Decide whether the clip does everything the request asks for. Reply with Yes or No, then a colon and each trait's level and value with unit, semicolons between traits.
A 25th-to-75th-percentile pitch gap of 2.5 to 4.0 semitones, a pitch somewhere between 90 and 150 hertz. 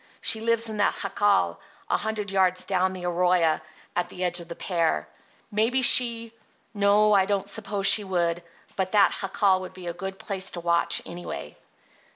No: average, 2.9 semitones; high, 190 Hz